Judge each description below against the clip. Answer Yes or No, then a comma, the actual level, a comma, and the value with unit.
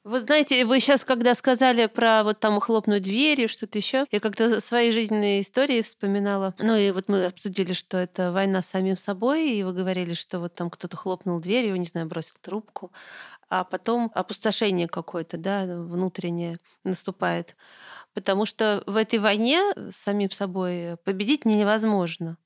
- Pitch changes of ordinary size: Yes, average, 3.5 semitones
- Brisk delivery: Yes, fast, 170 wpm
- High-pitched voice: Yes, high, 200 Hz